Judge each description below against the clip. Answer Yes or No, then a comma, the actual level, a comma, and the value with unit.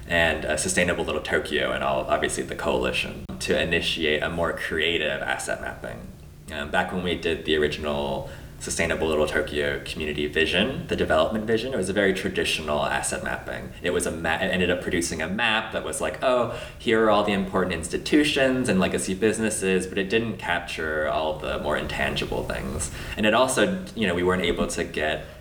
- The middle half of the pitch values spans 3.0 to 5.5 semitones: Yes, average, 4.5 semitones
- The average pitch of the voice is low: Yes, very low, 85 Hz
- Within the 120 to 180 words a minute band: No, average, 190 wpm